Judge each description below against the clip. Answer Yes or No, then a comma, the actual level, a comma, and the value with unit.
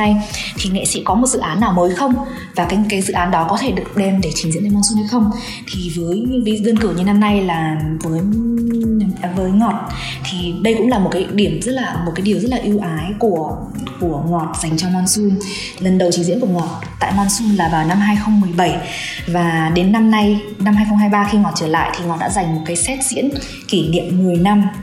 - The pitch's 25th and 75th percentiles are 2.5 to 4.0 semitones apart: Yes, average, 3.3 semitones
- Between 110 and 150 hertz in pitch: No, high, 195 Hz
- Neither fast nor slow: Yes, average, 230 wpm